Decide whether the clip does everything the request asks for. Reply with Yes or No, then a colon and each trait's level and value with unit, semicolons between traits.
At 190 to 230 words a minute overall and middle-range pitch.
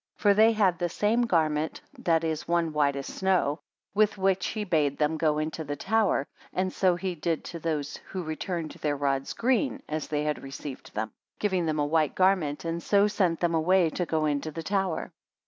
Yes: average, 200 wpm; medium, 165 Hz